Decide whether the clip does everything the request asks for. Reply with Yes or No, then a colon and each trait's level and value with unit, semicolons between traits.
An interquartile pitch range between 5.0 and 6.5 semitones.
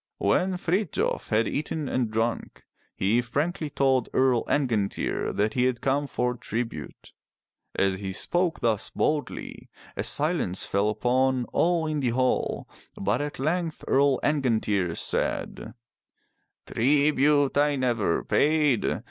No: average, 4.6 semitones